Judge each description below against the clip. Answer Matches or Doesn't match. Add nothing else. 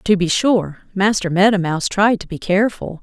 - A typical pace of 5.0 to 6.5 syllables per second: Matches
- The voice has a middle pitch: Doesn't match